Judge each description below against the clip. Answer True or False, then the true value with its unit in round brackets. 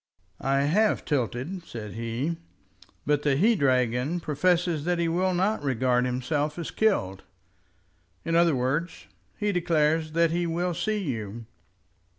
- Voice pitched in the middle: True (155 Hz)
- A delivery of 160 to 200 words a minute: False (140 wpm)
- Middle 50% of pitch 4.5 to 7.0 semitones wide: True (5.3 semitones)